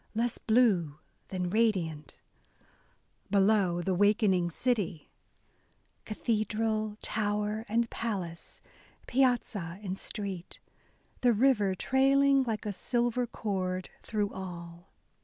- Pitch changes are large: No, average, 3.9 semitones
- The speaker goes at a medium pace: No, slow, 95 wpm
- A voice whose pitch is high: Yes, high, 210 Hz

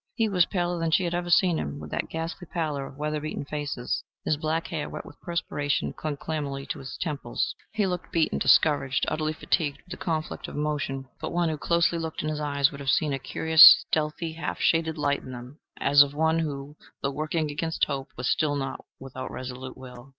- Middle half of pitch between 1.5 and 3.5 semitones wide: Yes, average, 2.8 semitones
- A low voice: No, medium, 150 Hz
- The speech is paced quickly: Yes, fast, 215 wpm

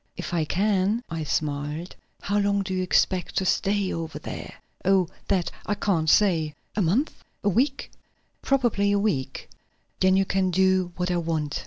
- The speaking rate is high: No, average, 170 wpm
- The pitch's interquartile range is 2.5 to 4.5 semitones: Yes, average, 3.4 semitones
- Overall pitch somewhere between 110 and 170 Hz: No, medium, 185 Hz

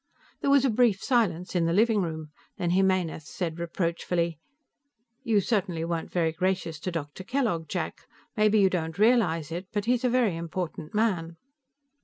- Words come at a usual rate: Yes, average, 170 wpm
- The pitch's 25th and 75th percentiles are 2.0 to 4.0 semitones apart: No, average, 4.4 semitones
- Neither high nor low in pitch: Yes, medium, 180 Hz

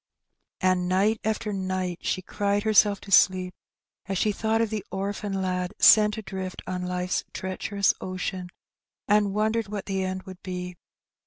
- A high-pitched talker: Yes, high, 195 Hz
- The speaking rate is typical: Yes, average, 155 wpm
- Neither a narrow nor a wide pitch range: No, narrow, 2.0 semitones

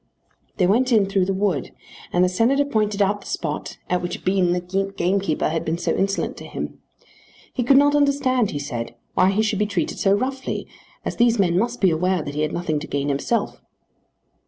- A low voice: No, high, 195 Hz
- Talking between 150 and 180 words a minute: No, fast, 205 wpm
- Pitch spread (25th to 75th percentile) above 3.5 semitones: Yes, average, 4.3 semitones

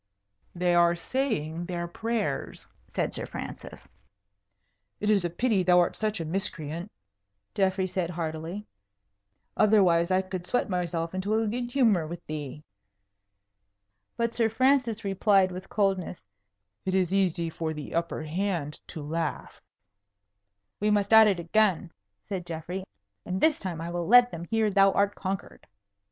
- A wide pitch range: No, average, 3.7 semitones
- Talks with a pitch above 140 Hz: Yes, medium, 185 Hz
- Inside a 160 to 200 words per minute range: No, average, 145 wpm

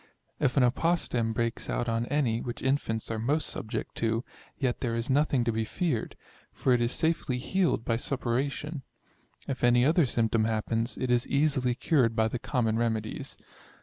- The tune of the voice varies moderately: Yes, average, 3.3 semitones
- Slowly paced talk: No, average, 175 wpm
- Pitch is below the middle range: Yes, low, 120 Hz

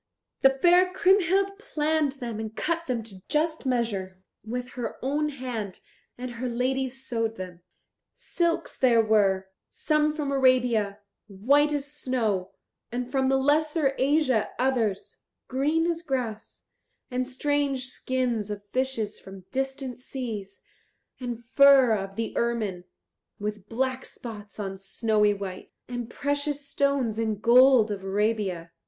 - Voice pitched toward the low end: No, very high, 250 Hz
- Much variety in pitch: No, average, 4.6 semitones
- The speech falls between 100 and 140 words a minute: Yes, slow, 135 wpm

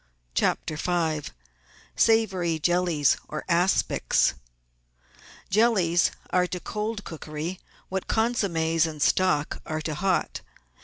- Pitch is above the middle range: No, medium, 175 Hz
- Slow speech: Yes, slow, 100 wpm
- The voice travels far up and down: No, average, 3.2 semitones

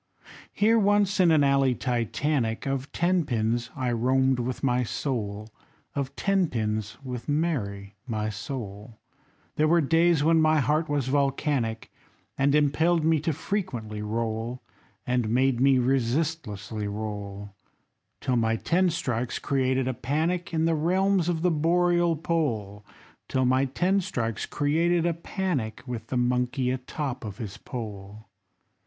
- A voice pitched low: Yes, low, 130 Hz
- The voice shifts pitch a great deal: Yes, wide, 5.9 semitones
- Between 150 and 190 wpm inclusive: No, average, 140 wpm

